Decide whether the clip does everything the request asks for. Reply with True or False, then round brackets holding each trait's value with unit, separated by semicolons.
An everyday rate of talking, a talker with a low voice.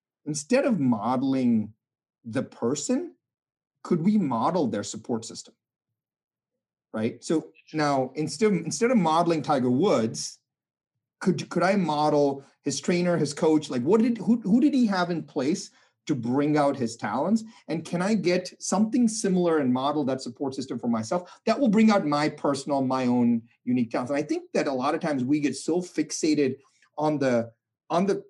False (175 wpm; 155 Hz)